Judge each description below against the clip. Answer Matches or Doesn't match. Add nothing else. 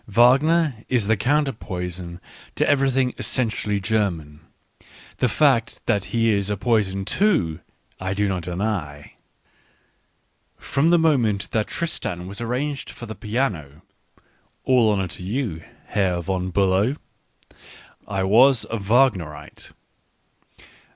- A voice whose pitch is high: Doesn't match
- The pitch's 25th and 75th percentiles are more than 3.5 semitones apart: Matches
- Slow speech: Matches